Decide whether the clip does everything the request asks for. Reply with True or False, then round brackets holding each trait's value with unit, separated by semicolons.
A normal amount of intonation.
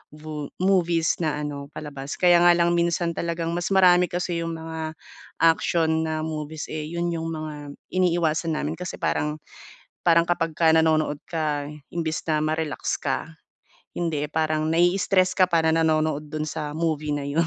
False (1.8 semitones)